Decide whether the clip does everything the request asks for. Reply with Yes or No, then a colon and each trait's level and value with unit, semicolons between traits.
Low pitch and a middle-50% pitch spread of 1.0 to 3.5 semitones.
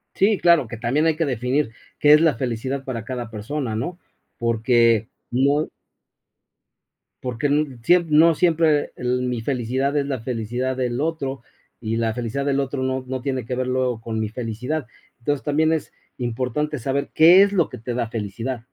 No: low, 130 Hz; average, 3.9 semitones